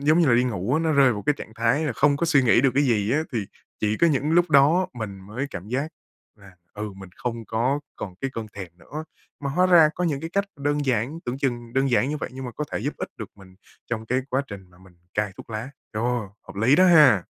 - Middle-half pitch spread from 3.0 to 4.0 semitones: No, average, 5.2 semitones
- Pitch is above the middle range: No, low, 125 Hz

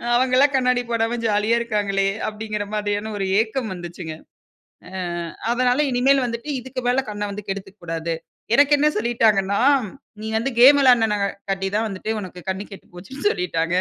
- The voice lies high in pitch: Yes, high, 215 Hz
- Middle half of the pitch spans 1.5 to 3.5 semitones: No, average, 4.0 semitones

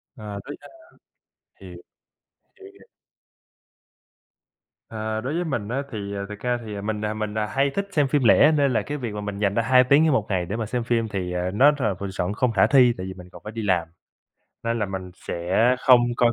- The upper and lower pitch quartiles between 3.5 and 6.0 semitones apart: Yes, average, 3.9 semitones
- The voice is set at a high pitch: No, low, 110 Hz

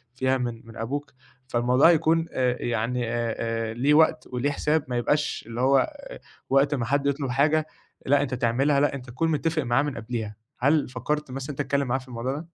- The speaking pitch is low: Yes, low, 130 Hz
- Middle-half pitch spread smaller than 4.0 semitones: Yes, average, 3.3 semitones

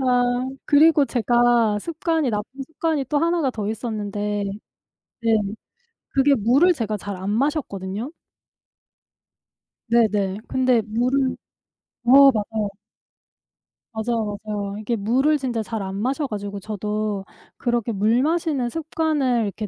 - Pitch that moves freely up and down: No, average, 4.6 semitones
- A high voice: Yes, high, 235 Hz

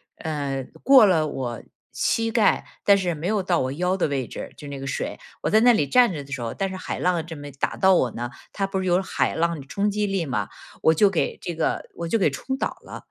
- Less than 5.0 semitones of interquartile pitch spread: No, wide, 5.6 semitones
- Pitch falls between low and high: Yes, medium, 170 Hz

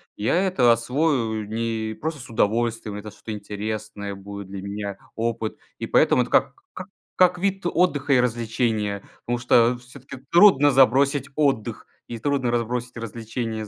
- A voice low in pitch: Yes, low, 115 Hz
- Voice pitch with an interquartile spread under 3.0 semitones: No, average, 4.1 semitones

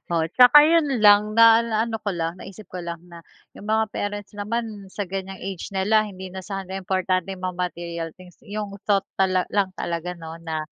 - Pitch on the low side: No, high, 195 Hz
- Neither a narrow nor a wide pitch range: Yes, average, 3.0 semitones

